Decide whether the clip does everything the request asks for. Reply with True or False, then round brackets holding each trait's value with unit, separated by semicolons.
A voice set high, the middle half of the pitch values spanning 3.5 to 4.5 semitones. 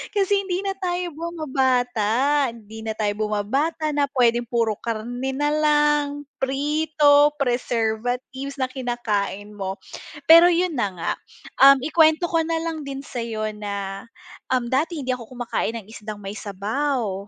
False (260 Hz; 5.2 semitones)